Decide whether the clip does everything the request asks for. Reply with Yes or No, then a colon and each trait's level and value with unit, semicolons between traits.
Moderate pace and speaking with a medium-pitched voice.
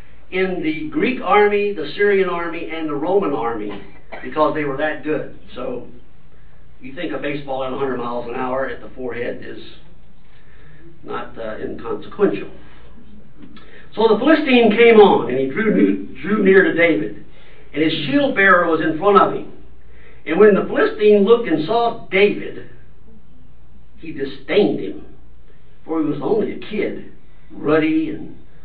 Yes: average, 155 wpm; medium, 160 Hz